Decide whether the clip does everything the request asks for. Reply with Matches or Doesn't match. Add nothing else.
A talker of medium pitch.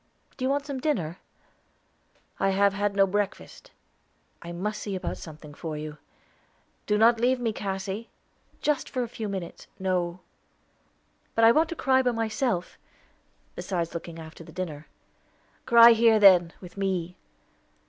Doesn't match